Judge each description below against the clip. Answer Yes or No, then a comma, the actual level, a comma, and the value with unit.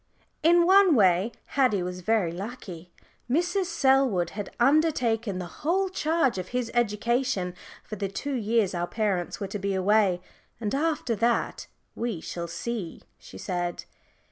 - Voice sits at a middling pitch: No, high, 220 Hz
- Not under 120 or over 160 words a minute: Yes, average, 145 wpm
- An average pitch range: No, wide, 6.4 semitones